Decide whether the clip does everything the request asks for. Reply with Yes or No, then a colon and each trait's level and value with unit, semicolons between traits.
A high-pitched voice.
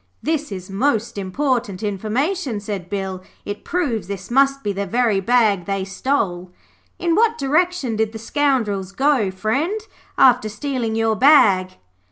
Yes: high, 220 Hz